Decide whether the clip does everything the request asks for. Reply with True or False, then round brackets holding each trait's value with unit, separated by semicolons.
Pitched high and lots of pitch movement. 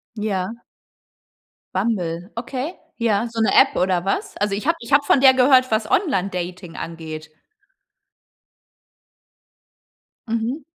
True (220 Hz; 6.0 semitones)